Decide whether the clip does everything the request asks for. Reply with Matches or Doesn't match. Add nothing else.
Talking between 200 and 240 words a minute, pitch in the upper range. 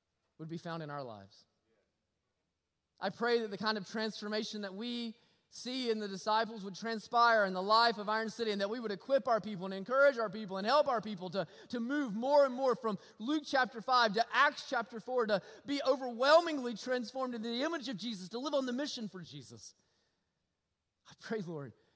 Matches